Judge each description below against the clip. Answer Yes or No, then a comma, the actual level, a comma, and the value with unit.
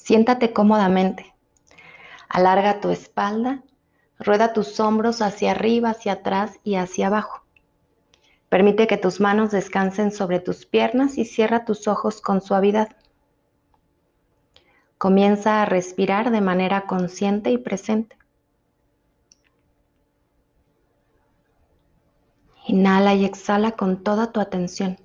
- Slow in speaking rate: Yes, slow, 105 wpm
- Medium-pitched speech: No, high, 205 Hz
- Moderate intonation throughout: No, narrow, 2.3 semitones